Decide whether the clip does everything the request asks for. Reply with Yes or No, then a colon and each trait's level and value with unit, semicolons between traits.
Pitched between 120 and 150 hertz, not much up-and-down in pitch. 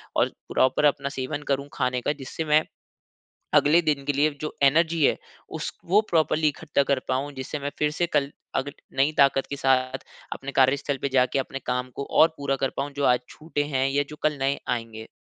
Yes: medium, 140 Hz; narrow, 2.1 semitones